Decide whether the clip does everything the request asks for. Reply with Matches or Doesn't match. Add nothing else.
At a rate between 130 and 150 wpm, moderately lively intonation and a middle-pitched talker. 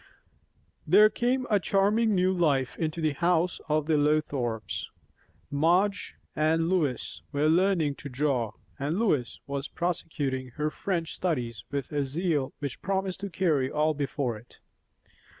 Matches